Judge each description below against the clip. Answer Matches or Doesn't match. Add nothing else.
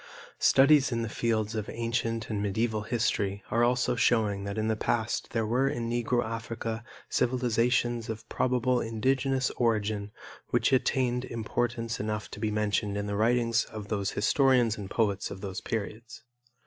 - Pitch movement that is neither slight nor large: Doesn't match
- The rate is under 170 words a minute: Matches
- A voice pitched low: Matches